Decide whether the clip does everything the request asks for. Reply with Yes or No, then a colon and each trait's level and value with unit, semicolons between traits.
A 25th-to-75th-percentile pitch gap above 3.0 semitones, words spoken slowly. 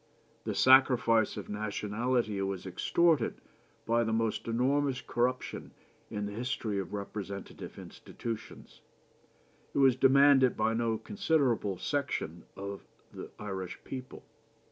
Yes: average, 4.2 semitones; slow, 115 wpm